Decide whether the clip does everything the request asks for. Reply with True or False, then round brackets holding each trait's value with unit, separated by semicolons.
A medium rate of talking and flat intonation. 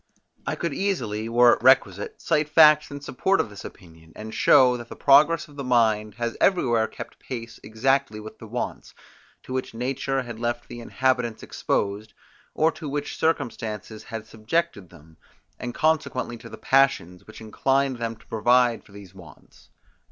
False (170 wpm; 4.0 semitones)